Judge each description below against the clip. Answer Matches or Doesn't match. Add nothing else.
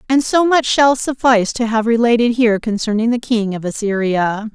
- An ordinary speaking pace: Matches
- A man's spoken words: Doesn't match